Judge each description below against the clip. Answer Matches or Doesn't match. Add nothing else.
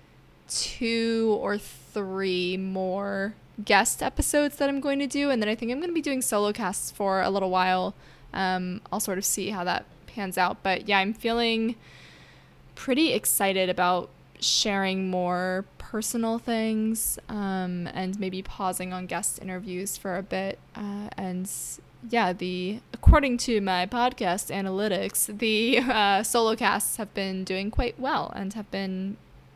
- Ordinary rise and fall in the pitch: Matches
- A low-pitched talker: Doesn't match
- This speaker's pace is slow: Doesn't match